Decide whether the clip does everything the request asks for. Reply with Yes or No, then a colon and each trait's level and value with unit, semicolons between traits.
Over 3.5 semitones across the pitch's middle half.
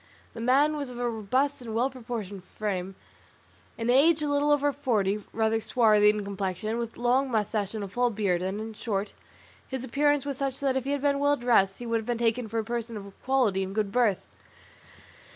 Yes: average, 4.1 semitones